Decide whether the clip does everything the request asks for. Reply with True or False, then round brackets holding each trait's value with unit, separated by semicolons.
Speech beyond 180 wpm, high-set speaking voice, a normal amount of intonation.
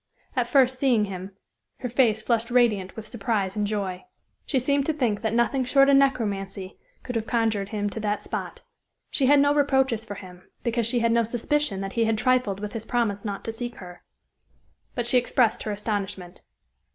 True (195 wpm; 225 Hz; 3.6 semitones)